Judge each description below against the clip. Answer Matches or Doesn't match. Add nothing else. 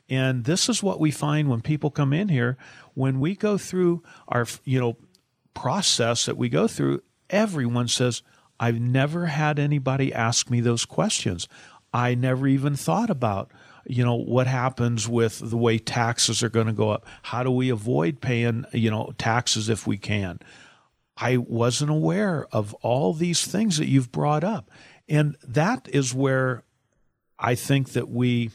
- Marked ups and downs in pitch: Doesn't match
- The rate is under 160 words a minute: Doesn't match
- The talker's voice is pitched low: Matches